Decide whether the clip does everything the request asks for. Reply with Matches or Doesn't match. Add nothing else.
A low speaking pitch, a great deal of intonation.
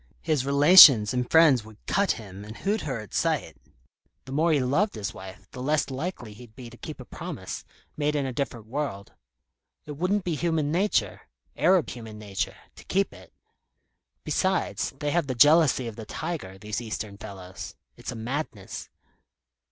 Matches